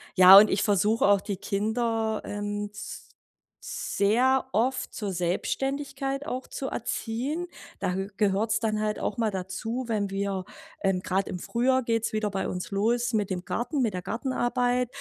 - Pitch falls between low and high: No, high, 215 Hz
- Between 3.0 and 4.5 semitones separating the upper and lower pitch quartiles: Yes, average, 3.6 semitones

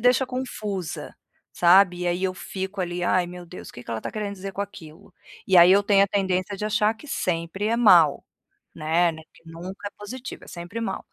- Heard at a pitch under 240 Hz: Yes, high, 190 Hz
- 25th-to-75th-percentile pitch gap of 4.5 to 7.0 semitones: No, average, 2.9 semitones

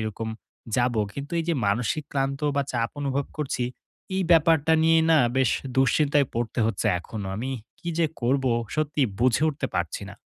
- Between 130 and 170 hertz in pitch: Yes, low, 135 Hz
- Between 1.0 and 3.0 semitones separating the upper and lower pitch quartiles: No, average, 4.2 semitones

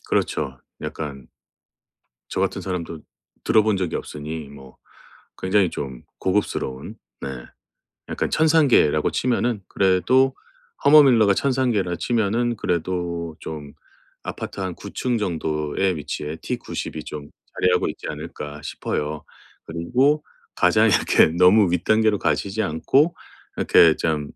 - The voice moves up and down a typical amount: No, wide, 6.2 semitones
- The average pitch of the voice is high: No, very low, 90 Hz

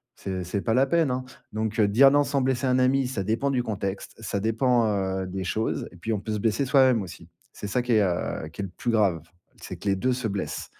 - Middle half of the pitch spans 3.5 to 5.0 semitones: Yes, average, 4.6 semitones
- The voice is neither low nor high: No, low, 110 Hz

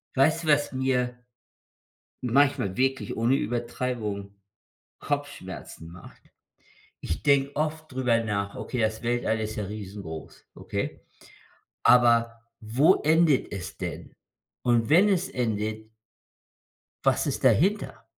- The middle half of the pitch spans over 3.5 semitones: Yes, average, 4.8 semitones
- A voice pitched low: Yes, low, 120 Hz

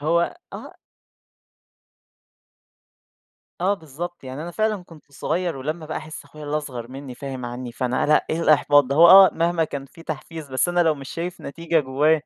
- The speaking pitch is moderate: Yes, medium, 155 Hz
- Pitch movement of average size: Yes, average, 3.6 semitones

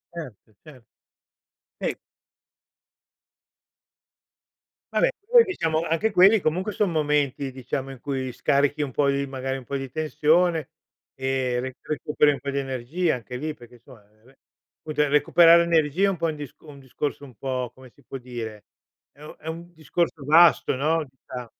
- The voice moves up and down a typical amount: Yes, average, 3.6 semitones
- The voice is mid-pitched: Yes, medium, 145 Hz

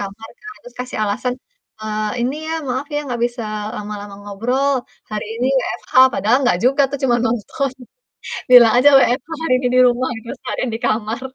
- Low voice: No, high, 240 Hz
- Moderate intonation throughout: Yes, average, 3.1 semitones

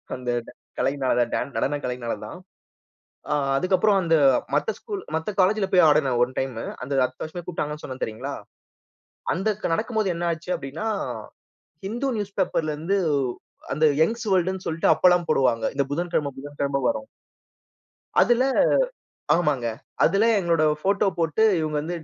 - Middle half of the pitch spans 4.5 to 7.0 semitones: Yes, wide, 5.4 semitones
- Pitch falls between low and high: Yes, medium, 165 Hz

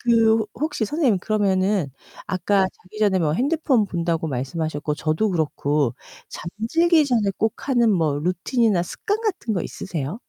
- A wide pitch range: Yes, wide, 6.0 semitones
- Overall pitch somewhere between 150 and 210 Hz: Yes, high, 200 Hz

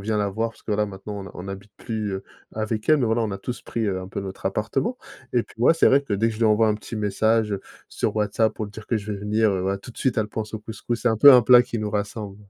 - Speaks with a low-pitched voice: Yes, low, 110 Hz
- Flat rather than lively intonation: Yes, narrow, 1.9 semitones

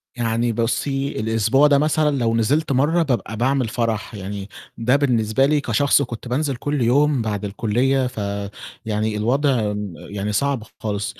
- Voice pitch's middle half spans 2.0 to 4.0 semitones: No, average, 4.6 semitones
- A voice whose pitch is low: Yes, low, 120 Hz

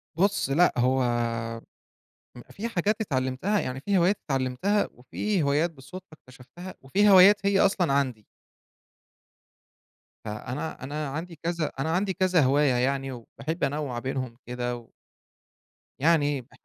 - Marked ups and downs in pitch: Yes, wide, 6.0 semitones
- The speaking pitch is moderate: Yes, medium, 145 Hz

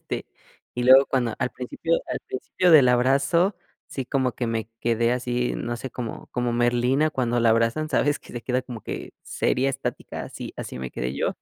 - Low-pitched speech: Yes, low, 125 Hz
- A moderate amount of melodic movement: No, narrow, 2.2 semitones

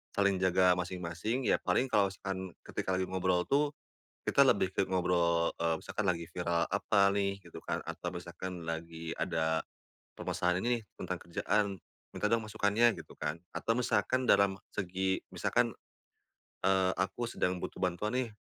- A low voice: Yes, very low, 95 Hz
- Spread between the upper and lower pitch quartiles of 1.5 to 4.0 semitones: Yes, average, 2.9 semitones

